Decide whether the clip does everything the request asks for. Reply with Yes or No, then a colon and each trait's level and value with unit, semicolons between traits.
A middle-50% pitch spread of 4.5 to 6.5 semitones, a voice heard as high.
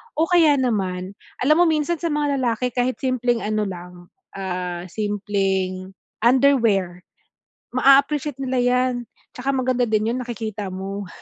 Yes: average, 5.3 semitones; high, 240 Hz